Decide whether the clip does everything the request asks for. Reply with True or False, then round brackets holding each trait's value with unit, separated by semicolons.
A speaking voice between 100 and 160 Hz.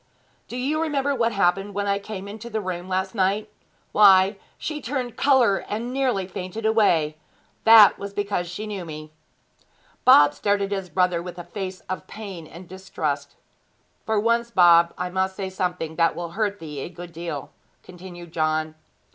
False (190 Hz)